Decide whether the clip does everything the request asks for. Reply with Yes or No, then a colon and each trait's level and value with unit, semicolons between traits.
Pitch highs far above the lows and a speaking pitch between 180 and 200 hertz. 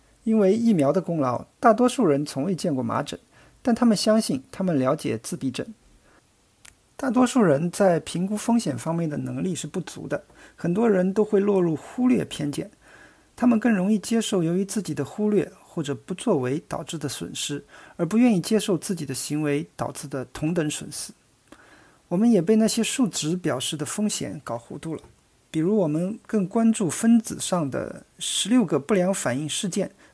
Yes: wide, 6.4 semitones; medium, 185 Hz